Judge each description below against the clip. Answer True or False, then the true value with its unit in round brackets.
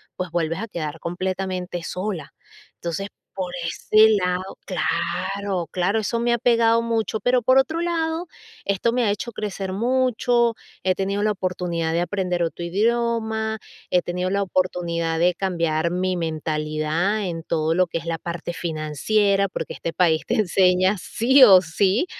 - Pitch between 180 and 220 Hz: True (185 Hz)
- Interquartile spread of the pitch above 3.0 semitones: True (4.2 semitones)